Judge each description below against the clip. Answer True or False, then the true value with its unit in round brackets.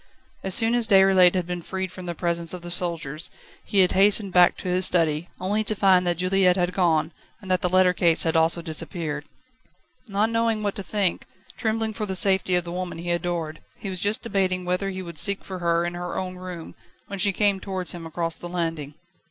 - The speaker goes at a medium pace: False (220 wpm)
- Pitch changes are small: True (2.1 semitones)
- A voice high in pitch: False (180 Hz)